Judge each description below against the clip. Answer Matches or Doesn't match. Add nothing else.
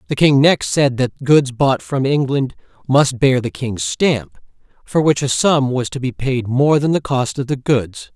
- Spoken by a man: Matches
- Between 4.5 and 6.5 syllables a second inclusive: Doesn't match